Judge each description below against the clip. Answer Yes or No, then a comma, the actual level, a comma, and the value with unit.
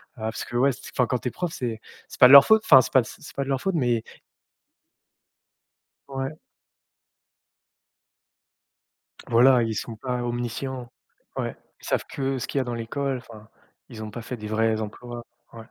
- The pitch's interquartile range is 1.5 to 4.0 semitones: Yes, average, 2.8 semitones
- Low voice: Yes, low, 120 Hz